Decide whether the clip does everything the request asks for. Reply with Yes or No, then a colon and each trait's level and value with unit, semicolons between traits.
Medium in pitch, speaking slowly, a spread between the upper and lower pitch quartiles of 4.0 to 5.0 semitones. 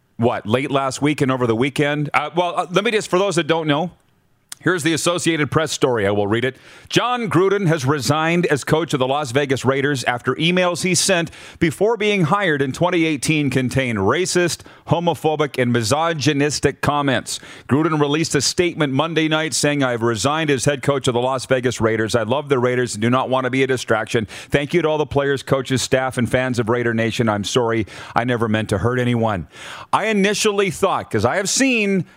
No: medium, 145 Hz; fast, 205 wpm; average, 4.6 semitones